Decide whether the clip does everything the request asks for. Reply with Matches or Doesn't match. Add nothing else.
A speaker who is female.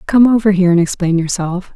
Matches